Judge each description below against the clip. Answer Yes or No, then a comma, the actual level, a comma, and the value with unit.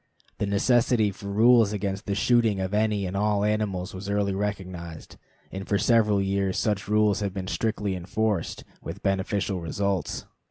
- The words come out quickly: No, average, 160 wpm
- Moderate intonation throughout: No, narrow, 1.7 semitones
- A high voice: No, low, 100 Hz